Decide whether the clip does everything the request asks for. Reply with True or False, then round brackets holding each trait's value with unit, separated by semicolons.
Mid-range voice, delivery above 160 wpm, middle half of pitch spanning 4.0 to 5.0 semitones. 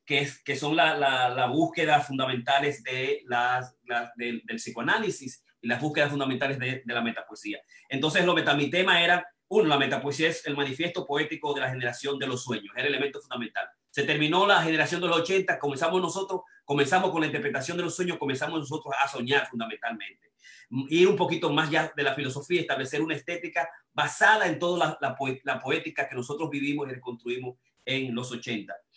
True (145 Hz; 190 wpm; 4.3 semitones)